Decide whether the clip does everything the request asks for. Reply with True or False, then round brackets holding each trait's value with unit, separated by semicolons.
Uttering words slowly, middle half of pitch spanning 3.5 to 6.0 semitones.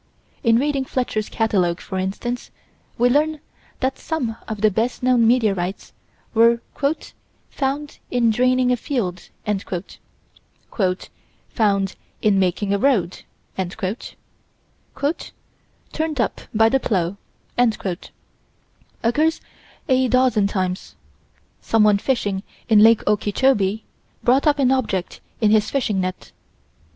True (105 wpm; 4.2 semitones)